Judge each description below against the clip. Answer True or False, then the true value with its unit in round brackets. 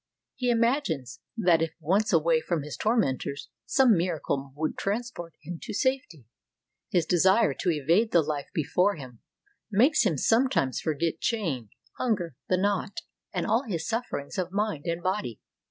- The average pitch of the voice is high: False (175 Hz)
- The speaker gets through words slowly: False (155 wpm)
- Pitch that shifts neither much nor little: False (5.8 semitones)